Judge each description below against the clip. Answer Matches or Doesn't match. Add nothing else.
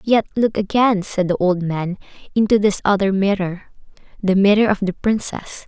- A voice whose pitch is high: Matches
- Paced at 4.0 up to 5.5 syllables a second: Matches